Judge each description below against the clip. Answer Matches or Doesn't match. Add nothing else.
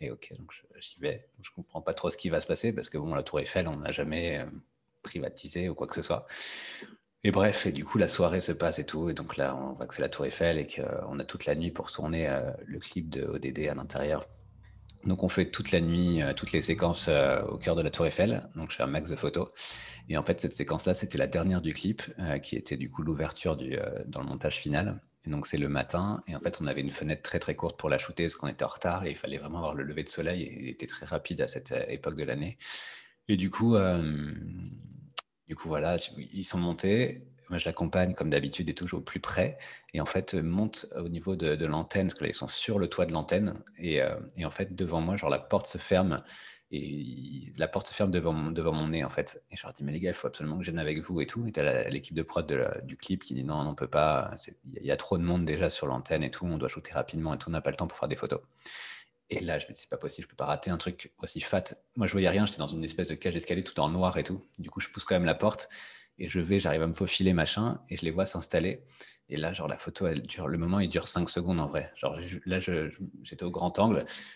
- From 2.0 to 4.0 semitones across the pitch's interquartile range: Matches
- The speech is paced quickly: Matches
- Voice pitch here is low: Matches